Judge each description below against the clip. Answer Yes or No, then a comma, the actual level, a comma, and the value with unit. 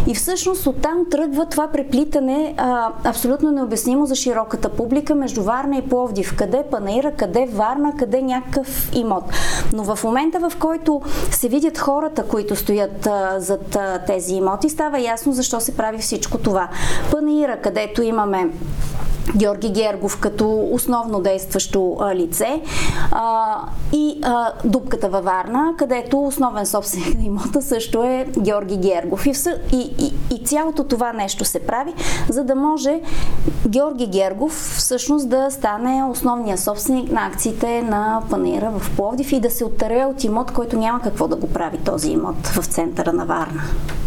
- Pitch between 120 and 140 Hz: No, high, 245 Hz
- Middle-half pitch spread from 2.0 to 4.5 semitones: No, average, 5.0 semitones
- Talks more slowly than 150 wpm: No, average, 155 wpm